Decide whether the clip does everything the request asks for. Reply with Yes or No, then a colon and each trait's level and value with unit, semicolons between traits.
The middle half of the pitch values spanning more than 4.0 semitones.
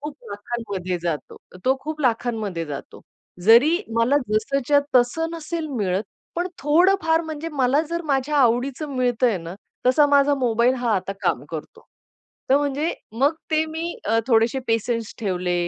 Yes: average, 5.0 semitones